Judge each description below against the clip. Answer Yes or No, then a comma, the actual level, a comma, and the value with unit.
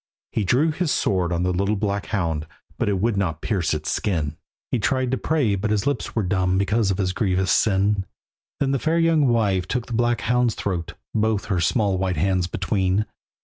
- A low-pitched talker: Yes, low, 100 Hz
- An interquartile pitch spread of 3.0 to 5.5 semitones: Yes, average, 4.1 semitones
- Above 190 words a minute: Yes, fast, 205 wpm